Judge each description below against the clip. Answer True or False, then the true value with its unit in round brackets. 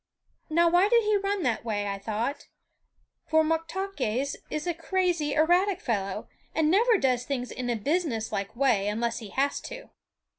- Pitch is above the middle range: True (295 Hz)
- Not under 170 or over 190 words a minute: False (160 wpm)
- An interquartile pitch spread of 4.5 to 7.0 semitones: False (7.4 semitones)